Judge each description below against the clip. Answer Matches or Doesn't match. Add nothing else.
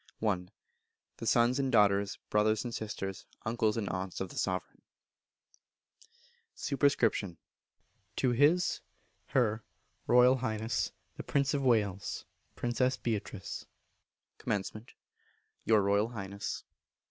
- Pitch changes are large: Doesn't match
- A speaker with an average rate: Doesn't match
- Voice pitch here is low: Matches